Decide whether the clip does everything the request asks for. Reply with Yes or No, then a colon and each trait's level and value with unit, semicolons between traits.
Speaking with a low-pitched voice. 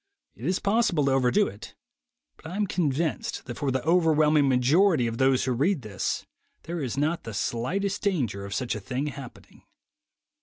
No: medium, 145 Hz